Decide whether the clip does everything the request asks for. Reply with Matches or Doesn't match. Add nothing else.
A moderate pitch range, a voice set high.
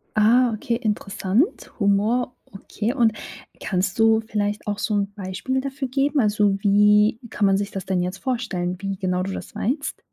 Matches